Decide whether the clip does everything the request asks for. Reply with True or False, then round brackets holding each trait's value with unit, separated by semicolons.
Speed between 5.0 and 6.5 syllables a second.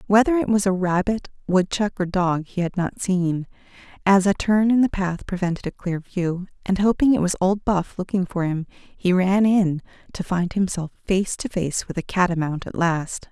False (4.8 syllables/s)